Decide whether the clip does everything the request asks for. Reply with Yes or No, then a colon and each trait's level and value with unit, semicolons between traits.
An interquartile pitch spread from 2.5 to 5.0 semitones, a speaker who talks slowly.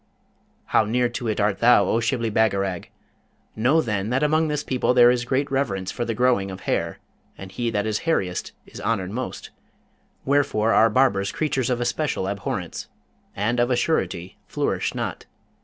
No: average, 4.2 semitones; average, 175 wpm